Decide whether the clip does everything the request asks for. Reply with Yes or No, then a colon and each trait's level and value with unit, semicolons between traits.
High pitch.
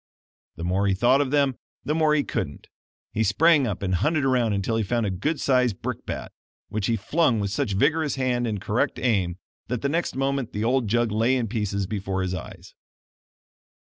No: low, 115 Hz